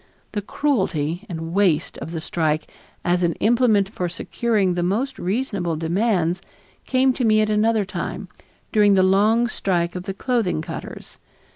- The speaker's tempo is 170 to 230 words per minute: No, average, 155 wpm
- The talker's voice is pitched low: No, high, 195 Hz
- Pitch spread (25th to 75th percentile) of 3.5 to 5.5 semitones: Yes, average, 4.3 semitones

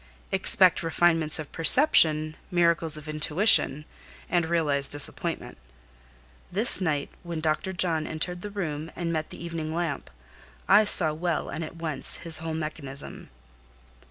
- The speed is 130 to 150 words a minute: Yes, average, 140 wpm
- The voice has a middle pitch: Yes, medium, 165 Hz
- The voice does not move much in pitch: Yes, narrow, 2.1 semitones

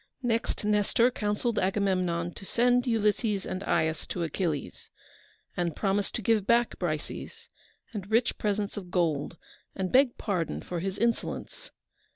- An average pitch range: Yes, average, 4.3 semitones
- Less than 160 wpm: Yes, average, 140 wpm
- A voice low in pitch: No, high, 200 Hz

